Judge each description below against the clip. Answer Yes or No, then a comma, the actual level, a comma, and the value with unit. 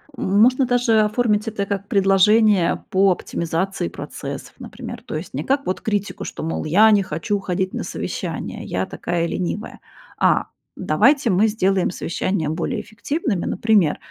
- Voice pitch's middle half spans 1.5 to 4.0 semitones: Yes, average, 3.5 semitones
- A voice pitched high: Yes, high, 195 Hz